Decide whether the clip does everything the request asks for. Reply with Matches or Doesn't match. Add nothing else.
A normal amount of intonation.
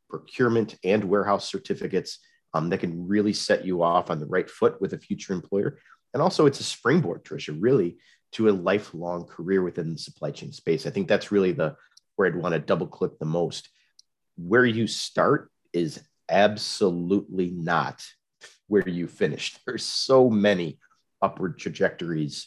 Matches